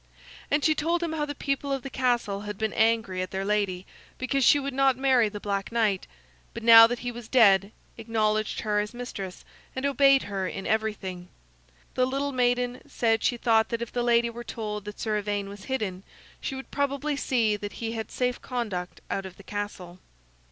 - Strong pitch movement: No, average, 3.9 semitones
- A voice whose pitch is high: Yes, high, 230 Hz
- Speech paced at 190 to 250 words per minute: Yes, fast, 205 wpm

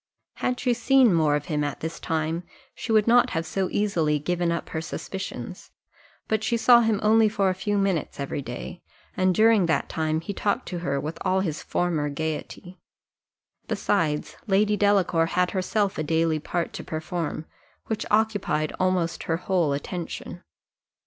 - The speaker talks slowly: No, average, 170 wpm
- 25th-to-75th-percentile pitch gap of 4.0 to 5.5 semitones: Yes, average, 4.5 semitones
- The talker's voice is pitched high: No, medium, 180 Hz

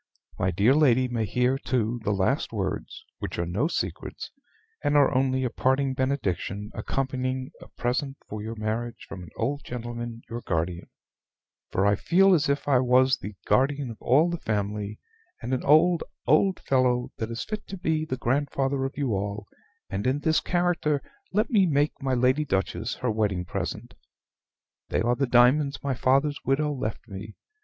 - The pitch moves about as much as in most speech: Yes, average, 4.5 semitones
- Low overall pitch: Yes, low, 130 Hz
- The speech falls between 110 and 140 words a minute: No, average, 175 wpm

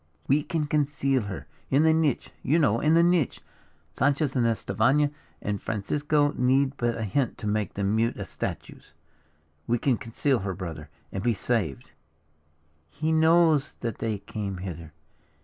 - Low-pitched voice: Yes, low, 125 Hz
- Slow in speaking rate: No, average, 160 wpm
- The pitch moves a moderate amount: No, wide, 6.1 semitones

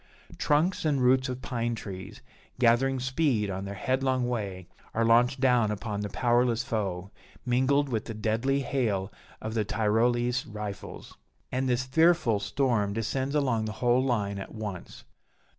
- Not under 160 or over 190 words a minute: No, average, 150 wpm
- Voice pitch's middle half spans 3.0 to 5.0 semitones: Yes, average, 3.6 semitones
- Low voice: Yes, low, 120 Hz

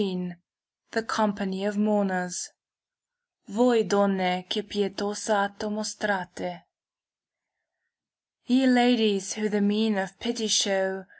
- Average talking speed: No, slow, 105 wpm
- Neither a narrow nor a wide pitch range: No, narrow, 2.0 semitones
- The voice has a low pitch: No, high, 205 Hz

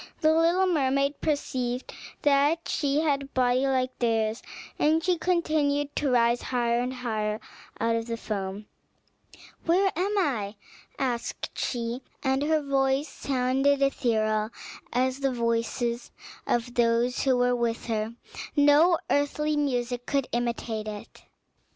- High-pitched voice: Yes, very high, 255 Hz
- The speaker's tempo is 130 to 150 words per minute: Yes, slow, 135 wpm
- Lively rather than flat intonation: No, average, 3.6 semitones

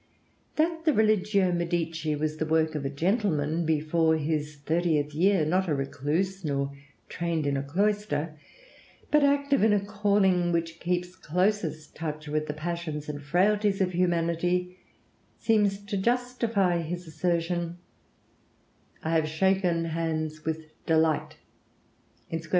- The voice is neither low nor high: Yes, medium, 170 Hz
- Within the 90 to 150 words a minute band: Yes, slow, 135 wpm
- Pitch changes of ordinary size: Yes, average, 3.7 semitones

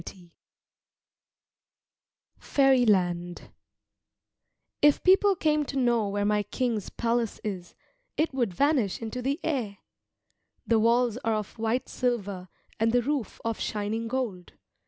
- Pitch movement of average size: Yes, average, 4.0 semitones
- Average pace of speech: No, slow, 120 wpm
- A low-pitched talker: No, high, 230 Hz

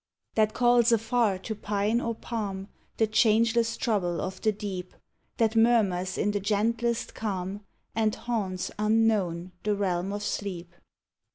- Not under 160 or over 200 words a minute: No, slow, 135 wpm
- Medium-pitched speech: No, high, 210 Hz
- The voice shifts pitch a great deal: No, average, 2.8 semitones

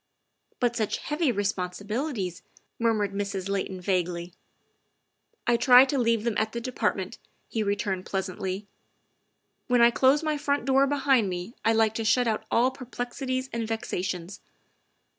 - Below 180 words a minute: Yes, average, 165 wpm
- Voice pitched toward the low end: No, high, 225 Hz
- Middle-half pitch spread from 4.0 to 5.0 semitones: Yes, average, 4.3 semitones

